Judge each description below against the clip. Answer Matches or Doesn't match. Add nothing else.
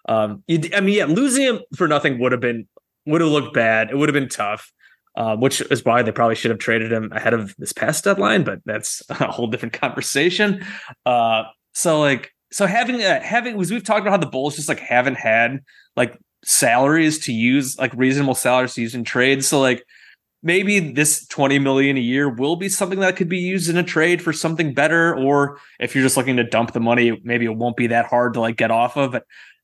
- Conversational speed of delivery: Doesn't match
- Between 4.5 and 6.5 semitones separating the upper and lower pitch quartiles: Matches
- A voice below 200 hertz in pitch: Matches